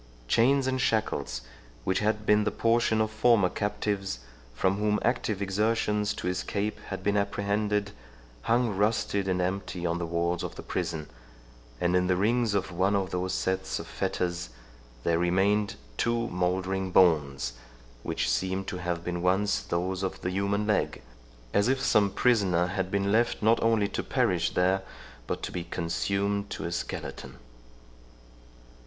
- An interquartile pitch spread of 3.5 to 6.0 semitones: No, average, 2.7 semitones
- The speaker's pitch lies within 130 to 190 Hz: No, low, 100 Hz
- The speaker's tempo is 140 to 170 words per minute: Yes, average, 160 wpm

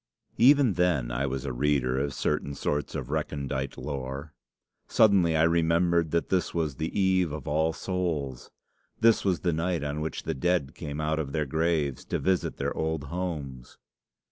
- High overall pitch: No, very low, 80 Hz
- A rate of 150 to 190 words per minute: Yes, average, 170 wpm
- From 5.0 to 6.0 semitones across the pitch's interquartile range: No, average, 3.7 semitones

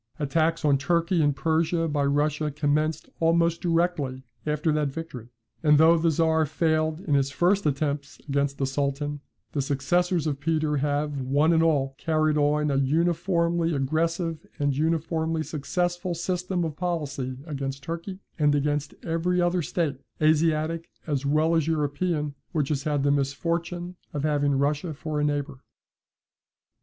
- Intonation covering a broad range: No, narrow, 2.6 semitones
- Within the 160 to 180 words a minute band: No, average, 150 wpm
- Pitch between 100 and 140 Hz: No, medium, 155 Hz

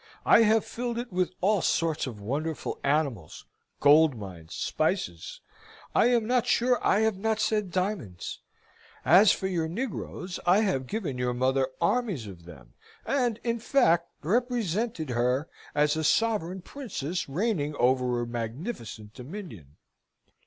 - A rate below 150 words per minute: Yes, average, 140 wpm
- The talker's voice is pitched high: No, medium, 170 Hz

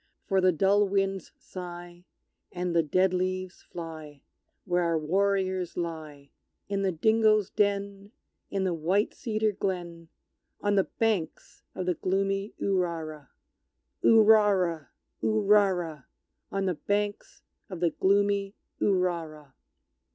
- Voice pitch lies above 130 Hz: Yes, medium, 185 Hz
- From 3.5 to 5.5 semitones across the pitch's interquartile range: No, average, 2.9 semitones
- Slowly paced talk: Yes, slow, 115 wpm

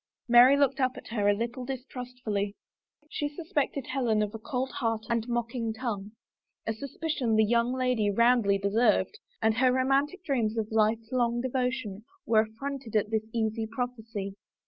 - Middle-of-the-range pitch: No, high, 235 Hz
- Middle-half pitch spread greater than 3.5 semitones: No, average, 2.8 semitones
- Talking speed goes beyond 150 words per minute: Yes, average, 170 wpm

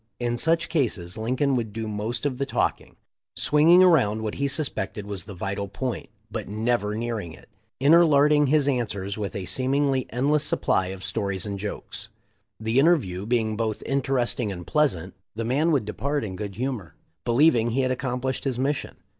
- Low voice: Yes, low, 120 Hz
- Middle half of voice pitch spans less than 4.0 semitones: No, average, 5.0 semitones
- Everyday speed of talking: Yes, average, 170 wpm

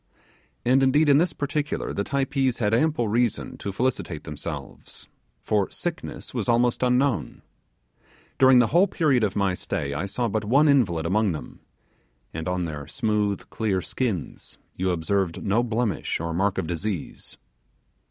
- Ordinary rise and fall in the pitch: No, wide, 6.2 semitones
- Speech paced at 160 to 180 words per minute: No, average, 150 wpm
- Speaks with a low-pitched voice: Yes, low, 110 Hz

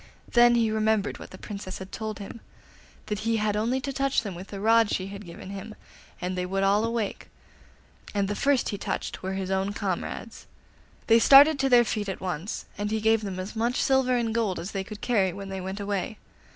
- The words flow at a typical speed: No, fast, 220 wpm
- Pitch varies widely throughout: No, average, 3.0 semitones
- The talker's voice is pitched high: Yes, high, 210 Hz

